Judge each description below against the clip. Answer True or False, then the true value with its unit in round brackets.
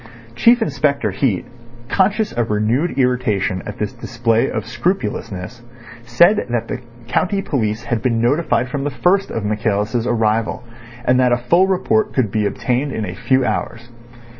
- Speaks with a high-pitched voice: False (120 Hz)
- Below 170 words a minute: True (160 wpm)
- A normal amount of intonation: True (4.5 semitones)